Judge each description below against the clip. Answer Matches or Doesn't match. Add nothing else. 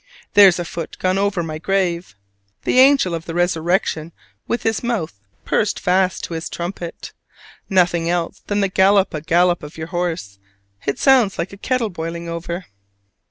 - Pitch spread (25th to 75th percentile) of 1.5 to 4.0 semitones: Matches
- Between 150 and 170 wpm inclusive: Matches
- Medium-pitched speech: Matches